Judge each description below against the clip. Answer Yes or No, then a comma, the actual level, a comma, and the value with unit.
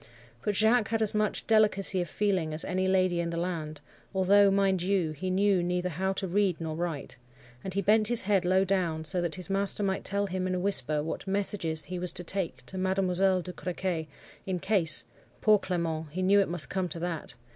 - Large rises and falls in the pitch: No, narrow, 2.6 semitones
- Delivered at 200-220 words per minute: Yes, fast, 205 wpm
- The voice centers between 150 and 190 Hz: Yes, medium, 185 Hz